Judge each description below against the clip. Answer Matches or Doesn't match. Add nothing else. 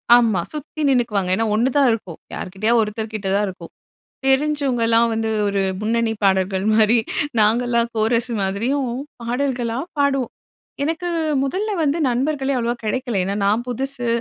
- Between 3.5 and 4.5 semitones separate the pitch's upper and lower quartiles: Matches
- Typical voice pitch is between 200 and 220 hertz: Doesn't match